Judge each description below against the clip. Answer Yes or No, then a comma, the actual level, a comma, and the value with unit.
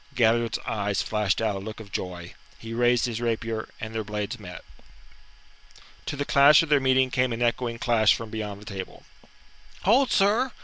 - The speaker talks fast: No, average, 180 wpm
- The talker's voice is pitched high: No, low, 115 Hz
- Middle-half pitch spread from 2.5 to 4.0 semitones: Yes, average, 3.3 semitones